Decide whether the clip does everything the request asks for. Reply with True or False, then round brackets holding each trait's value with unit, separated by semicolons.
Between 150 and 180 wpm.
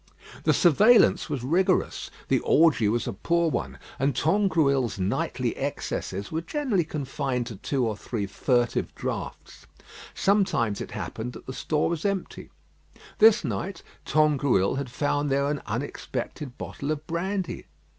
False (140 wpm)